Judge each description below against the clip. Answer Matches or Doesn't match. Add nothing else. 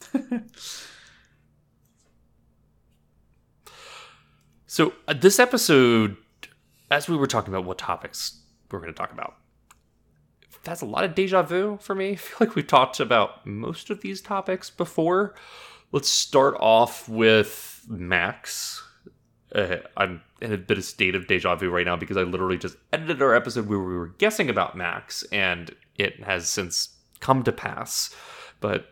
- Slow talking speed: Doesn't match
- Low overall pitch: Matches